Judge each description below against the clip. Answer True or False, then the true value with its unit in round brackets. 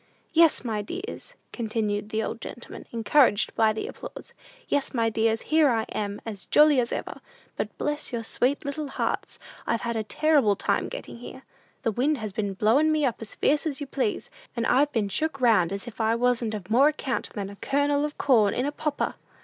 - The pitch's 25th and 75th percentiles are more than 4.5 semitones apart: True (4.9 semitones)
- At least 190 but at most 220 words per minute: True (205 wpm)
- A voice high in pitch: True (240 Hz)